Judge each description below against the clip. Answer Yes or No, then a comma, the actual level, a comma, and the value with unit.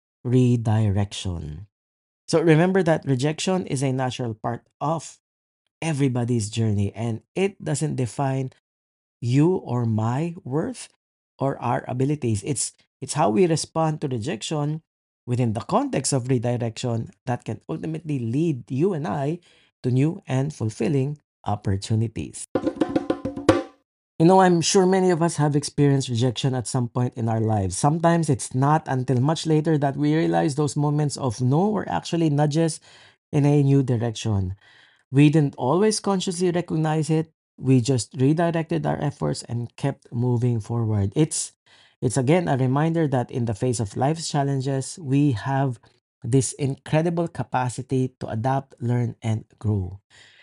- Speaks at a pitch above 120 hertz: Yes, low, 135 Hz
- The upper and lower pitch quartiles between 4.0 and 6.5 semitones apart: Yes, average, 4.8 semitones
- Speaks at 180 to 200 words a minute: No, average, 145 wpm